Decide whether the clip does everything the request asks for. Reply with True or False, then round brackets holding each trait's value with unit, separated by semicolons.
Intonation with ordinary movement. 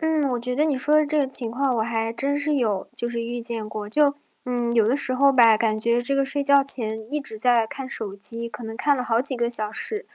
True (3.6 semitones)